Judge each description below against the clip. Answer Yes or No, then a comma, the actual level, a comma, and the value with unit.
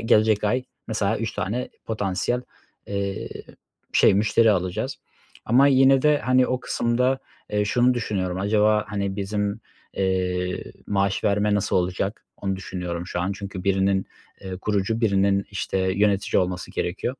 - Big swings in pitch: No, average, 2.7 semitones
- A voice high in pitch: No, low, 100 Hz